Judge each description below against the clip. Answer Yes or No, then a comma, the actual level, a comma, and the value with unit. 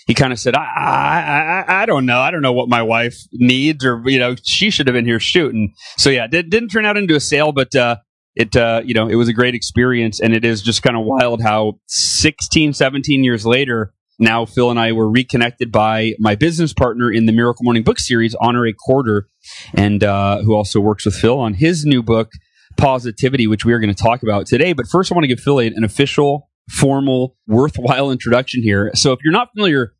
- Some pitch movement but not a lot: Yes, average, 3.5 semitones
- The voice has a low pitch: Yes, low, 120 Hz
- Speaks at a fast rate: Yes, fast, 230 wpm